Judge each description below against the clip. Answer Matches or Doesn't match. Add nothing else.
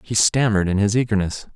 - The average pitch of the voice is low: Matches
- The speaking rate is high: Doesn't match